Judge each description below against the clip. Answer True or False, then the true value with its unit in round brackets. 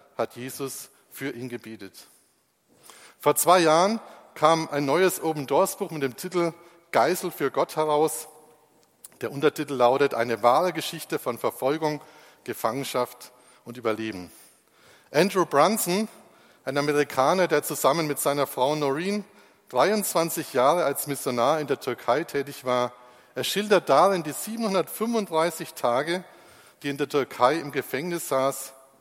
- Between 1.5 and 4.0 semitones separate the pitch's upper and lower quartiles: False (4.5 semitones)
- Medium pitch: True (150 Hz)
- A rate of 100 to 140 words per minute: True (130 wpm)